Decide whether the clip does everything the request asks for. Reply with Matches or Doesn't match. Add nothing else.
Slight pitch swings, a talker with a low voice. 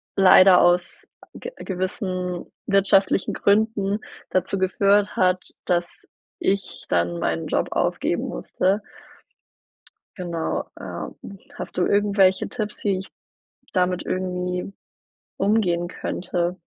Doesn't match